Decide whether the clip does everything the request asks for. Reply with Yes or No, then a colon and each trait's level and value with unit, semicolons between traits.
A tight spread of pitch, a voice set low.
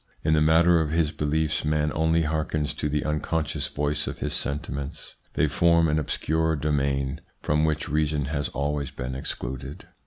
Yes: narrow, 1.5 semitones; very low, 75 Hz